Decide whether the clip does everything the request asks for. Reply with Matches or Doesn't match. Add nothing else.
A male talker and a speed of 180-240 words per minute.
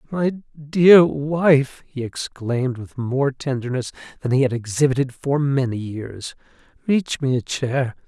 Doesn't match